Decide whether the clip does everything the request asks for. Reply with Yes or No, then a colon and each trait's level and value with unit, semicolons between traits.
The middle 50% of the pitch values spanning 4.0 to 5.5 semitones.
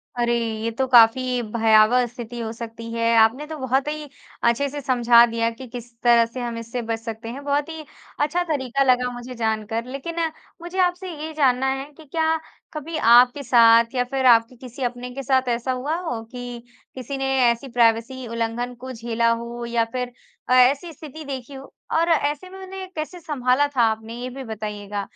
No: average, 3.2 semitones